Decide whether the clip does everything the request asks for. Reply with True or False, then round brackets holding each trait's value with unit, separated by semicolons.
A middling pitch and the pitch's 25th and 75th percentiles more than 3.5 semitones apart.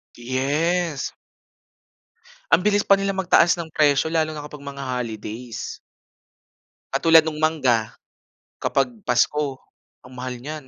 True (150 Hz; 4.2 semitones)